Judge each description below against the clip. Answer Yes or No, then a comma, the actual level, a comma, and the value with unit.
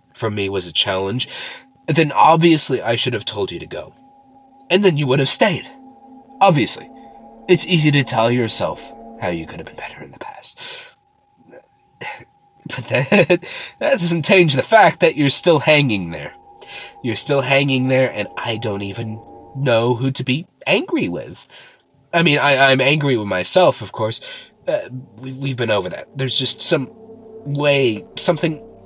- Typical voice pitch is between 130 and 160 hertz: Yes, low, 135 Hz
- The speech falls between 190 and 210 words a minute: No, average, 170 wpm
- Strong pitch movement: Yes, wide, 6.9 semitones